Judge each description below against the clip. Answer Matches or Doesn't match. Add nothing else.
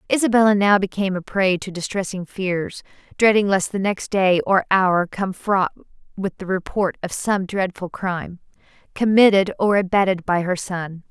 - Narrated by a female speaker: Matches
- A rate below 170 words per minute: Matches